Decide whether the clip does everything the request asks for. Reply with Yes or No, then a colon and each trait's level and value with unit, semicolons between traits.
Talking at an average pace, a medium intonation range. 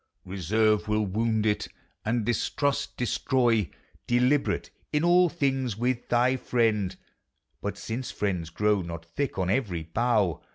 No: slow, 130 wpm; average, 4.2 semitones